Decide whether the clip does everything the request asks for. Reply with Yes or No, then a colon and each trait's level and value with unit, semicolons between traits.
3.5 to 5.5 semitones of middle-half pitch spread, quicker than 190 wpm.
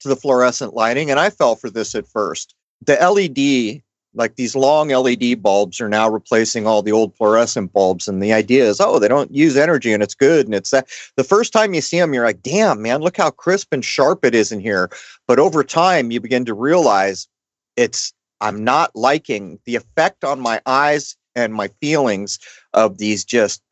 Yes: average, 4.2 semitones; fast, 205 wpm